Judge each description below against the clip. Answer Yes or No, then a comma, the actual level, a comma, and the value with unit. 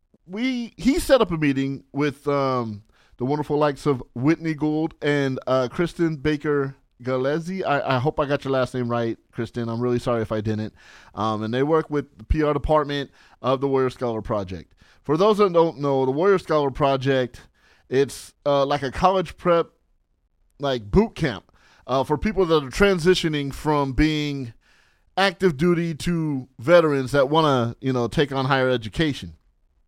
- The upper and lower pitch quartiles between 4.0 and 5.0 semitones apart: Yes, average, 4.4 semitones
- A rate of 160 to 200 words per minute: Yes, average, 175 wpm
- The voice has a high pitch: No, medium, 140 Hz